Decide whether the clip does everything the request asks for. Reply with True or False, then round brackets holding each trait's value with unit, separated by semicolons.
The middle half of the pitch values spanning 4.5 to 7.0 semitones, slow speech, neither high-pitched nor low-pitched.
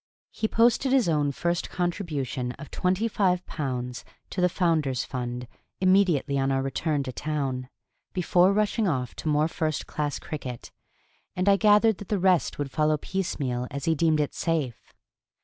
False (5.3 semitones; 165 wpm; 155 Hz)